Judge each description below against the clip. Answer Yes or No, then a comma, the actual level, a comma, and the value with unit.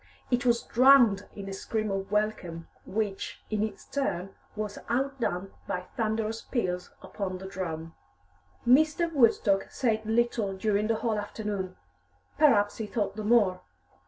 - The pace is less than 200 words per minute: Yes, average, 140 wpm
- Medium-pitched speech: No, high, 215 Hz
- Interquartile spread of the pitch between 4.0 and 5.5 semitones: No, average, 3.3 semitones